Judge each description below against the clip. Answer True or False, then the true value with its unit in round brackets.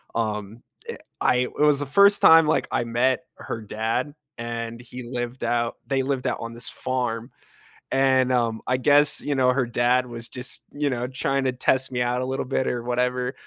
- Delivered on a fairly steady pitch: True (2.0 semitones)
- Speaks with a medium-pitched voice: False (125 Hz)